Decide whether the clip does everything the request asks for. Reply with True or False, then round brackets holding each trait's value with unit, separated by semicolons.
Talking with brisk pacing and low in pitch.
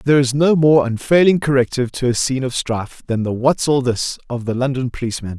True (225 wpm; 130 Hz)